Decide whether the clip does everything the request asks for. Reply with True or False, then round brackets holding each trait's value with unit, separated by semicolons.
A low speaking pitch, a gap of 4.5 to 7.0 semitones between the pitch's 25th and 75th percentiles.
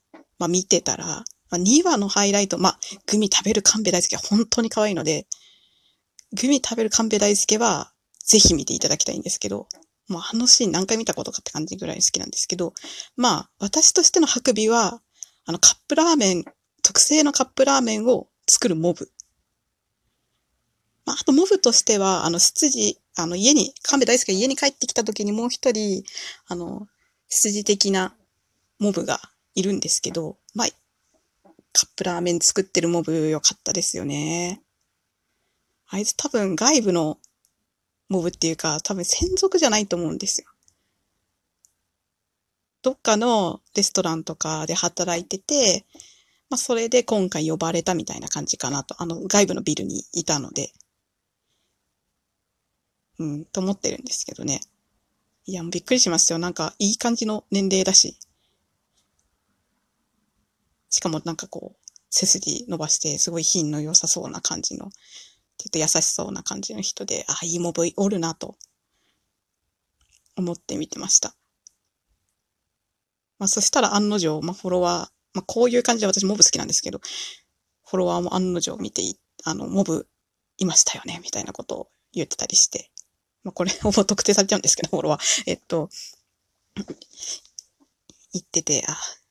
False (195 Hz; 5.3 semitones)